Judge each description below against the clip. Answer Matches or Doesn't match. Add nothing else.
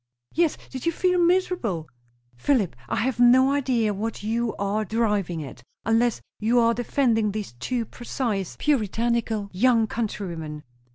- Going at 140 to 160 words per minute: Matches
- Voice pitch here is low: Doesn't match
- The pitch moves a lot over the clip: Doesn't match